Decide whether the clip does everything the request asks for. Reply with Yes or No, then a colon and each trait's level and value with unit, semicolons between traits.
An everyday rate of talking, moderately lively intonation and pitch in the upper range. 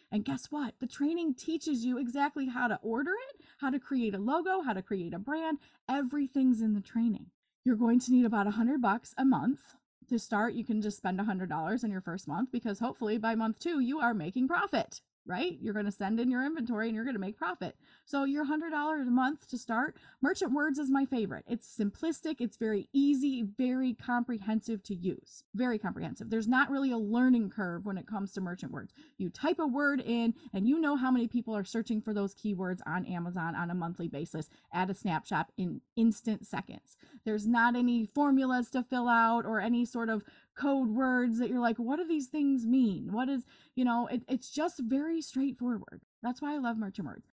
No: fast, 215 wpm; average, 4.1 semitones; high, 240 Hz